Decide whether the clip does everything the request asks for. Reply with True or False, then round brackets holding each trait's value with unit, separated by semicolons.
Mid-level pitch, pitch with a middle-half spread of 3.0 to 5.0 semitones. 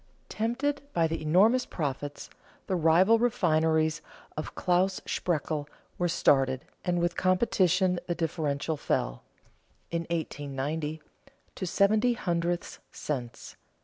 True (170 Hz; 3.4 semitones)